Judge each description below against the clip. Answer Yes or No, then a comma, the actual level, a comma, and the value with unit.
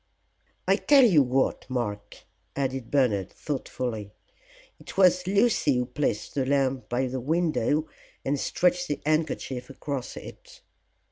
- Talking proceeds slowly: Yes, slow, 130 wpm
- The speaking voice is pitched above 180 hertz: No, low, 135 Hz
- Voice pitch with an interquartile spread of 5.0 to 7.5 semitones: No, average, 4.0 semitones